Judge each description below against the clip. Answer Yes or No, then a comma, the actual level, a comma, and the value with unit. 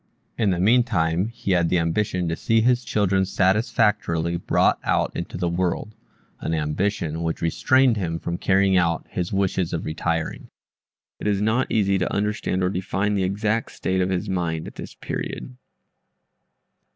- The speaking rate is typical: Yes, average, 165 wpm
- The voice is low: Yes, very low, 95 Hz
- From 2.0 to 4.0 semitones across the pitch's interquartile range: Yes, average, 3.5 semitones